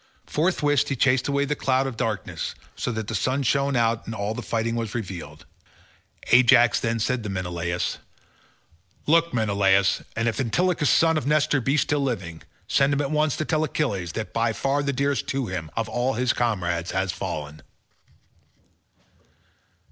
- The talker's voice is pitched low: Yes, low, 120 Hz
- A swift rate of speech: No, average, 170 wpm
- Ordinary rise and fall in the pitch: No, wide, 5.7 semitones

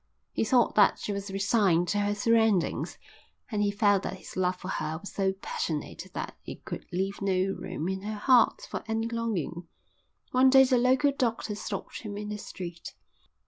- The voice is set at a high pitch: Yes, high, 205 Hz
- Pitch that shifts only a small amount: No, average, 3.0 semitones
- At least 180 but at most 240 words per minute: Yes, average, 185 wpm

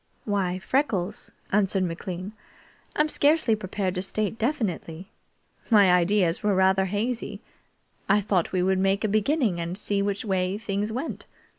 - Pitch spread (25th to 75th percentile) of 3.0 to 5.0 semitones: No, narrow, 2.6 semitones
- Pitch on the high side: Yes, high, 200 Hz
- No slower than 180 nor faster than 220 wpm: No, average, 145 wpm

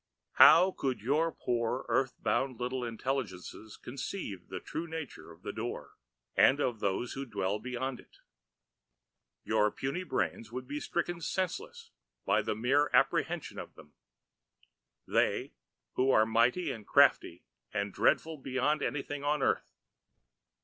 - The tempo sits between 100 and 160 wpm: Yes, slow, 135 wpm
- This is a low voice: Yes, low, 130 Hz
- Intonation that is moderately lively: Yes, average, 4.8 semitones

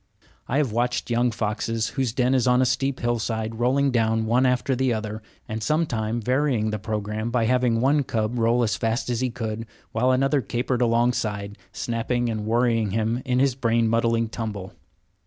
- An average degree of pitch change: No, narrow, 2.1 semitones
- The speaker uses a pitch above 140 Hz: No, low, 115 Hz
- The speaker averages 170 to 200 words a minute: Yes, average, 185 wpm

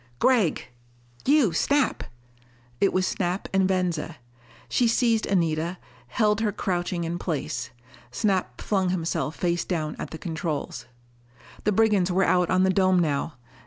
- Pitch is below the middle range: No, medium, 185 Hz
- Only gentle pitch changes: No, average, 3.2 semitones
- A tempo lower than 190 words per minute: Yes, average, 140 wpm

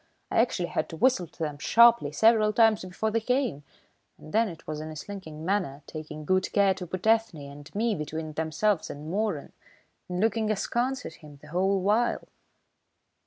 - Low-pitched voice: No, medium, 185 Hz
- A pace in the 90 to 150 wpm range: No, average, 185 wpm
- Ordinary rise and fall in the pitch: No, wide, 5.9 semitones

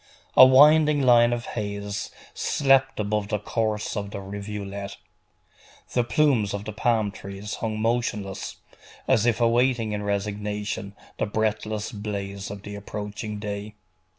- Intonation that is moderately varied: No, narrow, 2.3 semitones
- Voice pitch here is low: Yes, low, 105 Hz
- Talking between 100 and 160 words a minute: Yes, slow, 135 wpm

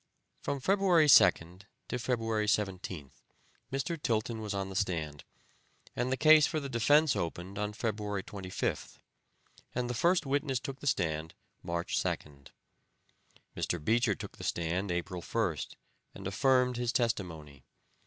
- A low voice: Yes, low, 105 Hz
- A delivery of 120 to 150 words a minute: Yes, average, 140 wpm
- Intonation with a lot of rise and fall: Yes, wide, 6.4 semitones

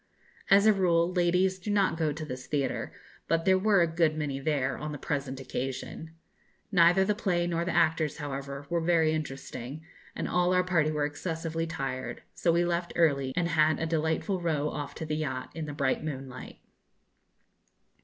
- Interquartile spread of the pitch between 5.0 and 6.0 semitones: No, average, 3.1 semitones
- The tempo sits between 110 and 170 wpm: No, average, 185 wpm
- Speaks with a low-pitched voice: No, medium, 160 Hz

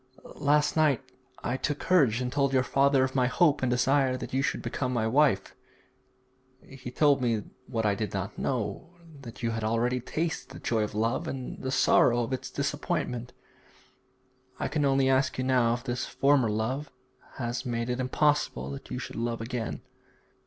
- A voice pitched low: Yes, low, 130 Hz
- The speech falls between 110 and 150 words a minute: No, average, 180 wpm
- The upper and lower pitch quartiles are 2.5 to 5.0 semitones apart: Yes, average, 2.9 semitones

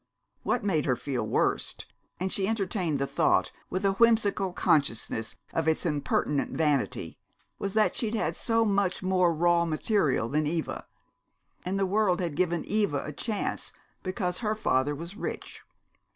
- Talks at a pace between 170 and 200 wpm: No, average, 155 wpm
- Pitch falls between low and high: Yes, medium, 180 Hz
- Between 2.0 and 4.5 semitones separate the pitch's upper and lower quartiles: No, average, 4.9 semitones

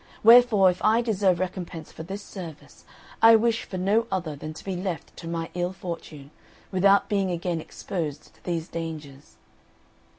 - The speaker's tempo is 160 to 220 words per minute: Yes, average, 165 wpm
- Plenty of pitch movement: No, average, 3.4 semitones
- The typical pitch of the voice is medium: Yes, medium, 180 Hz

